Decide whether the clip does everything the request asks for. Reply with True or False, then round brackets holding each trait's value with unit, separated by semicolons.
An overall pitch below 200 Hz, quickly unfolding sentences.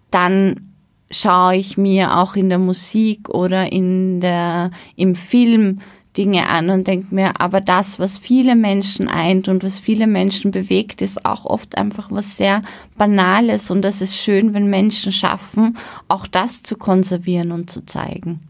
False (190 Hz; 160 wpm)